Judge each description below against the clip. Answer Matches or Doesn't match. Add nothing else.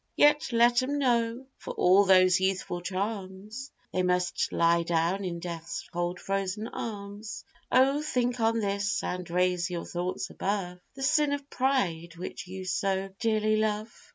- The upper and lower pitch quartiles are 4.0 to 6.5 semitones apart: Matches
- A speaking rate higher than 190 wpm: Doesn't match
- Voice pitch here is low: Doesn't match